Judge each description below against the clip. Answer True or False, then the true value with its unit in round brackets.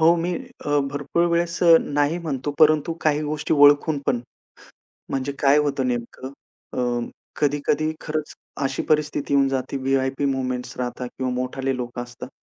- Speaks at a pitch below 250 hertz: True (140 Hz)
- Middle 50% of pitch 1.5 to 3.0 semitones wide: True (2.7 semitones)